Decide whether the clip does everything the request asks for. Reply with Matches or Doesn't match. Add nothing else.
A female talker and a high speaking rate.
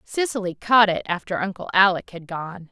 Doesn't match